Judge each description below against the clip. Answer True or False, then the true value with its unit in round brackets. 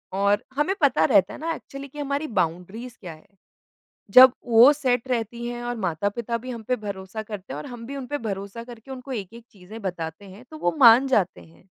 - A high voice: True (230 Hz)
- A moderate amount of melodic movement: True (4.4 semitones)